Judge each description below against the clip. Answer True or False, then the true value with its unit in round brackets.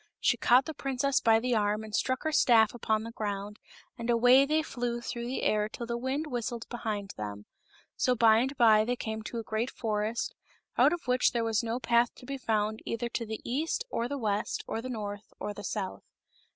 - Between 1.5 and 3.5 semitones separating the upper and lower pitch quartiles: True (2.5 semitones)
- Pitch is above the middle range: True (230 Hz)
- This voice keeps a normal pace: False (215 wpm)